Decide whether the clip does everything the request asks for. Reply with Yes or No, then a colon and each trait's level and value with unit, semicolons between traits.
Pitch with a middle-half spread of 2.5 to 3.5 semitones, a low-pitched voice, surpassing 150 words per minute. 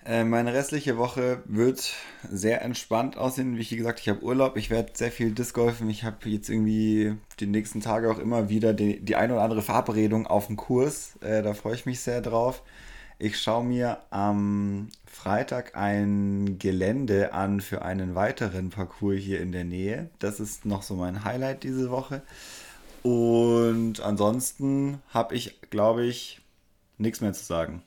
Yes: average, 3.0 semitones; low, 110 Hz; average, 165 wpm